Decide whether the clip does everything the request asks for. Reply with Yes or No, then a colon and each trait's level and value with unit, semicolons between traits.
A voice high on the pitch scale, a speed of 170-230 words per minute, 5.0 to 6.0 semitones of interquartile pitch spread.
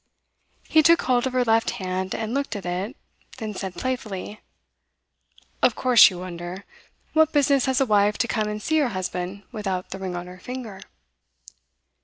Yes: high, 215 Hz; average, 175 wpm; average, 5.3 semitones